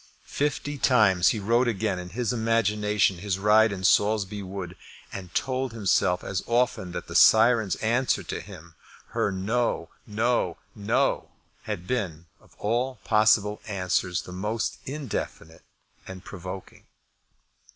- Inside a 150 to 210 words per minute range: No, slow, 135 wpm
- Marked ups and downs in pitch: No, average, 3.9 semitones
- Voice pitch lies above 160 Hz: No, low, 105 Hz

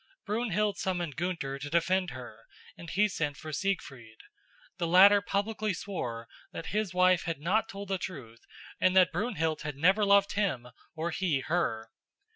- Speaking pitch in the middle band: Yes, medium, 180 Hz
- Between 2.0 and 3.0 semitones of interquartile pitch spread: No, average, 5.1 semitones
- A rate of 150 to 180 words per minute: Yes, average, 160 wpm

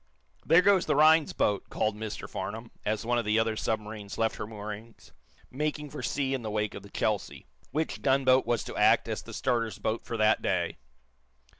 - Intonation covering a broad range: No, average, 3.9 semitones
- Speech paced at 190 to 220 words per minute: Yes, average, 195 wpm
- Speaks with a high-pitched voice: No, low, 115 Hz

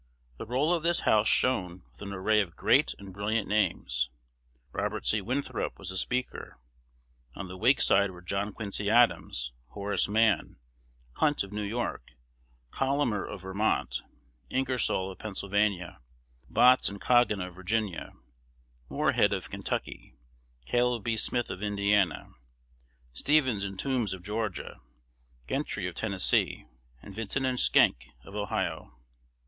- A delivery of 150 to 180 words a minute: No, slow, 135 wpm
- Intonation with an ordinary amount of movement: Yes, average, 4.0 semitones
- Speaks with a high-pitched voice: No, low, 105 Hz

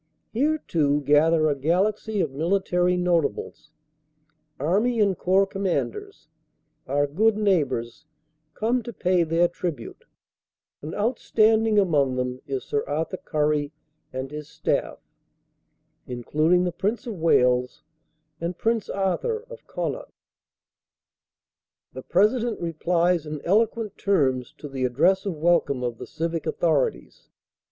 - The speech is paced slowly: Yes, slow, 125 wpm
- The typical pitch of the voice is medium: Yes, medium, 170 Hz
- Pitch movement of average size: No, wide, 5.7 semitones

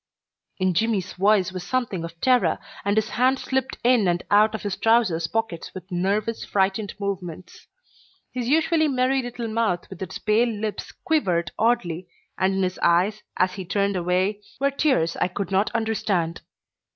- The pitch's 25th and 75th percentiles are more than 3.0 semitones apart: Yes, average, 4.1 semitones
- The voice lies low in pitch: No, high, 205 Hz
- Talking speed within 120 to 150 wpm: No, average, 165 wpm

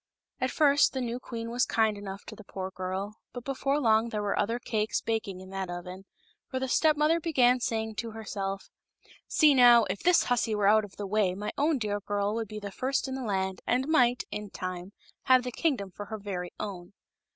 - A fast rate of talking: Yes, fast, 220 wpm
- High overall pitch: Yes, high, 220 Hz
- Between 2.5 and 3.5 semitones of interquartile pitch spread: No, average, 4.1 semitones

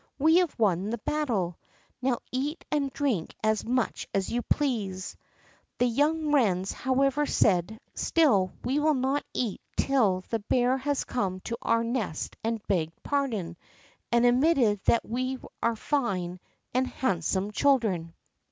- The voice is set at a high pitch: Yes, high, 235 Hz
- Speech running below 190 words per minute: Yes, average, 145 wpm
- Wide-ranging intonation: Yes, wide, 5.7 semitones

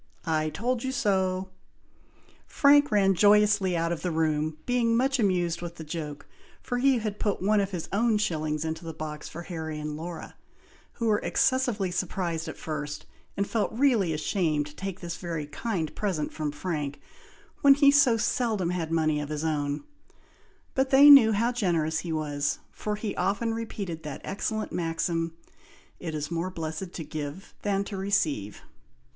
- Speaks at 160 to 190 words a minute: Yes, average, 170 wpm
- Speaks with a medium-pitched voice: Yes, medium, 180 Hz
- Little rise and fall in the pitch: No, average, 5.2 semitones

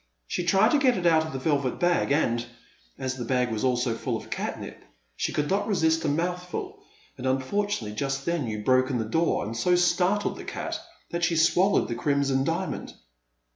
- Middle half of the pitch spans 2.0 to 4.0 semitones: No, wide, 5.6 semitones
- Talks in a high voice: No, medium, 150 Hz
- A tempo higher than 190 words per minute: Yes, average, 200 wpm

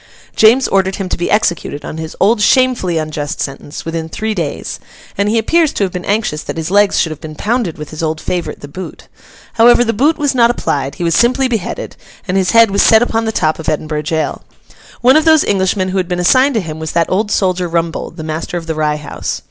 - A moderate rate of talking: No, fast, 235 wpm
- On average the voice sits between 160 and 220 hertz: Yes, medium, 185 Hz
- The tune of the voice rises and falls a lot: Yes, wide, 6.0 semitones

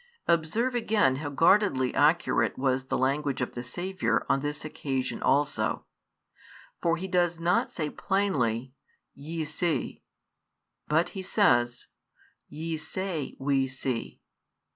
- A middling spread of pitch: Yes, average, 4.8 semitones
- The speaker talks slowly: Yes, slow, 120 wpm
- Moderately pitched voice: Yes, medium, 150 Hz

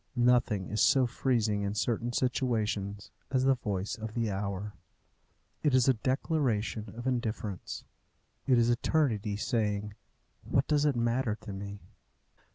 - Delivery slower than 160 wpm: Yes, average, 140 wpm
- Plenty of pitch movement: No, average, 3.6 semitones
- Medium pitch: No, low, 115 Hz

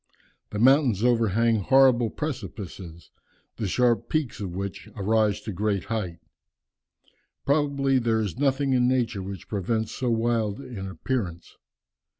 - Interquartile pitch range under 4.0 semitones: No, average, 4.3 semitones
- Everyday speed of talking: No, slow, 130 wpm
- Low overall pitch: Yes, low, 115 Hz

